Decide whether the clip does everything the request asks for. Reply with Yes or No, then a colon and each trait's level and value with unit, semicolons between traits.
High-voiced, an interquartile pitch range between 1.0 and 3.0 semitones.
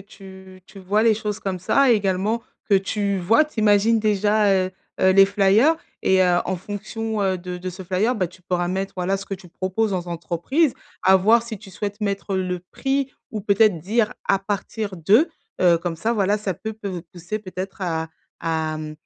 Yes: high, 195 Hz; average, 2.7 semitones